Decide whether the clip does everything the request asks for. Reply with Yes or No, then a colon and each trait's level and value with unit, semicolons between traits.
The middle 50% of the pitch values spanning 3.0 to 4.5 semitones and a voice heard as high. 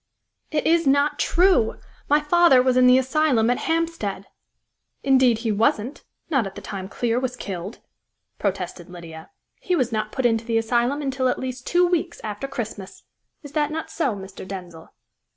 No: wide, 5.6 semitones; very high, 250 Hz